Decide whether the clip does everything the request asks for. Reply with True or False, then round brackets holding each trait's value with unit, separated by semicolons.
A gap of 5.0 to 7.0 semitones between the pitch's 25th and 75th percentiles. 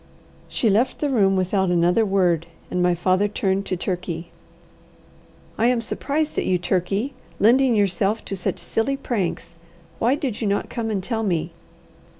False (4.2 semitones)